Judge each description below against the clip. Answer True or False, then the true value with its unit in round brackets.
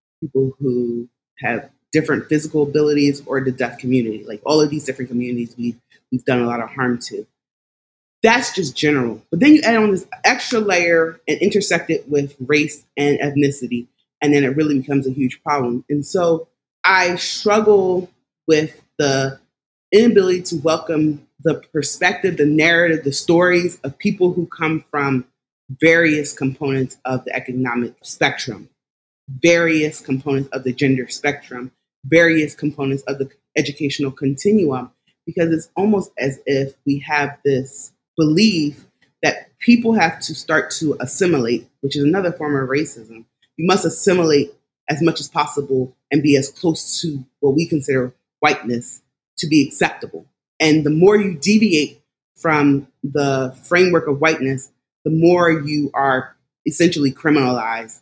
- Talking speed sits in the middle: True (150 wpm)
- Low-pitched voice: False (145 Hz)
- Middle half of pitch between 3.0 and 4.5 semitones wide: True (3.8 semitones)